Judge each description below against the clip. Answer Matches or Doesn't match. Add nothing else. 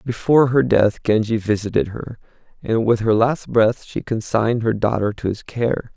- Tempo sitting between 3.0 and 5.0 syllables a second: Matches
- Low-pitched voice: Matches